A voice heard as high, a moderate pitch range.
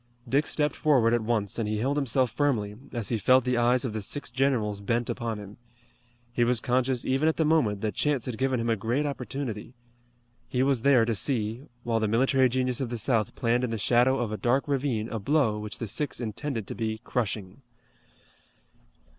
No: low, 120 Hz; average, 3.3 semitones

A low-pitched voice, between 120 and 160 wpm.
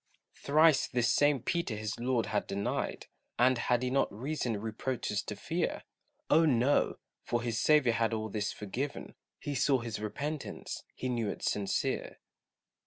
Yes: low, 120 Hz; average, 155 wpm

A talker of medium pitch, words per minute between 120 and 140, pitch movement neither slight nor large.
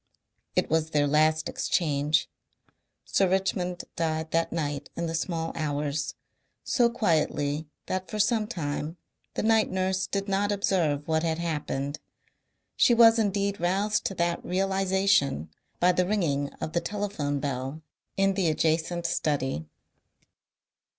Yes: medium, 170 Hz; slow, 135 wpm; average, 4.4 semitones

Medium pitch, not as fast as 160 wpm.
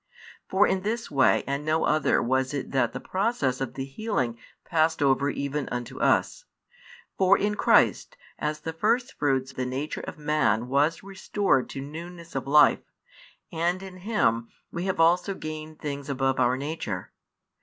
No: medium, 150 Hz; average, 165 wpm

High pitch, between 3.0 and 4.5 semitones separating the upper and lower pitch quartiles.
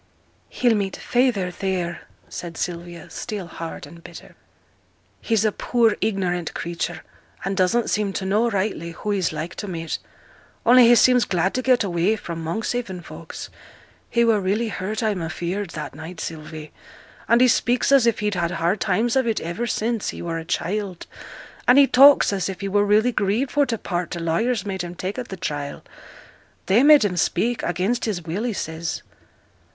No: high, 195 Hz; average, 4.9 semitones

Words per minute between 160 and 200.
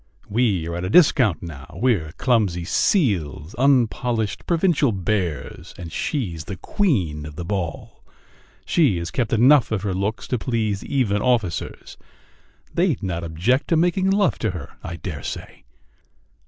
No: average, 150 wpm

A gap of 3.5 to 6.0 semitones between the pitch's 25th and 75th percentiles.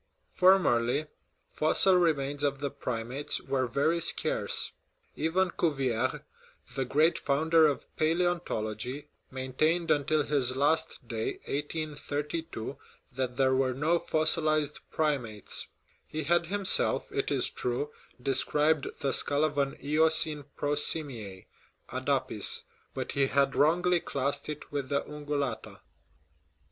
No: average, 3.0 semitones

